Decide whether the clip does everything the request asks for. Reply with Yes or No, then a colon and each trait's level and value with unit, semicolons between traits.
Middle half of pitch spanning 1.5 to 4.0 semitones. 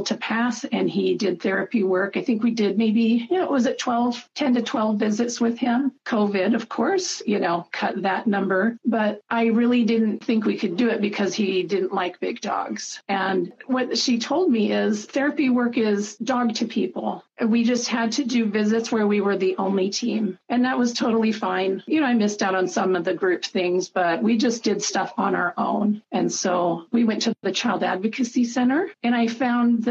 Yes: average, 3.6 semitones